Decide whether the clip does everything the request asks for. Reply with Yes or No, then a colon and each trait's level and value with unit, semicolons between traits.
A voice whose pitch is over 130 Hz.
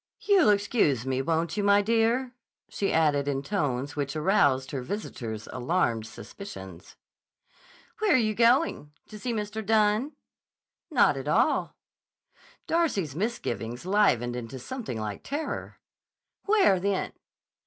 Yes: high, 190 Hz